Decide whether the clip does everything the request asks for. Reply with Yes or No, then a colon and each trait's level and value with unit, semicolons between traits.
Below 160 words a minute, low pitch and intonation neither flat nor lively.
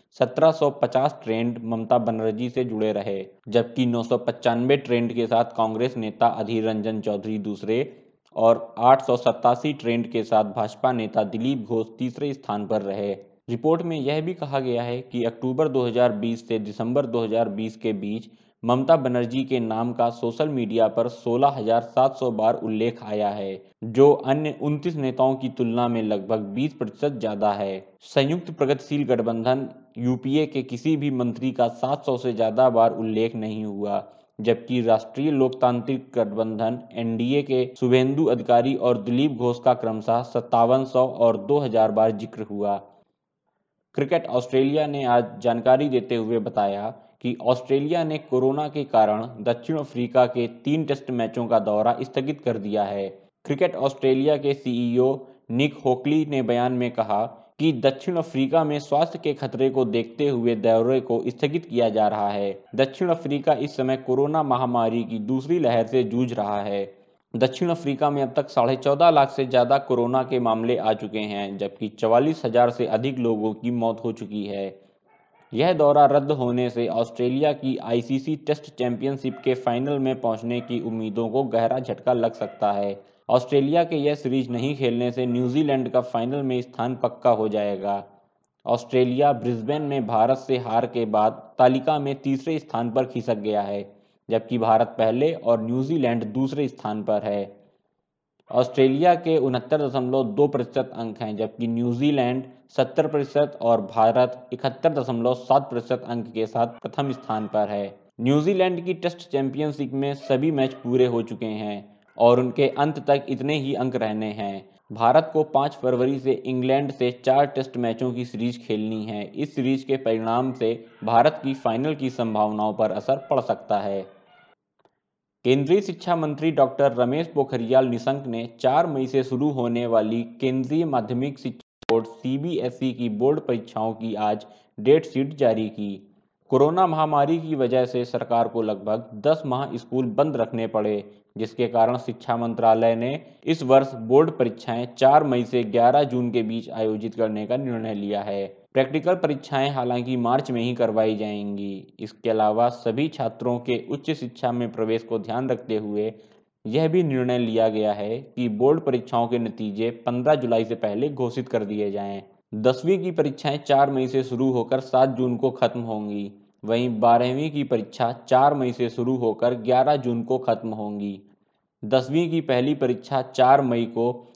No: average, 165 wpm; low, 125 Hz; average, 3.1 semitones